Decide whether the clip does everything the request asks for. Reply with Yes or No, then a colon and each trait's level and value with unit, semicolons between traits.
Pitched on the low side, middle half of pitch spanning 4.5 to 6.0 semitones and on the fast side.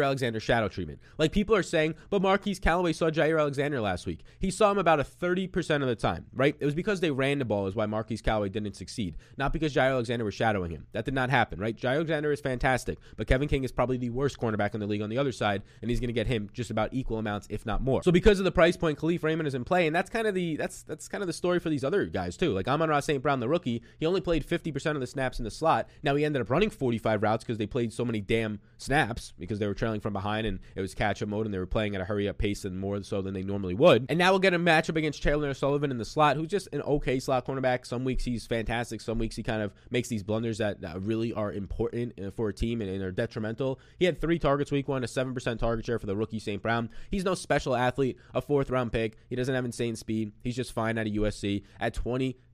Yes: low, 125 Hz; average, 5.3 semitones; fast, 280 wpm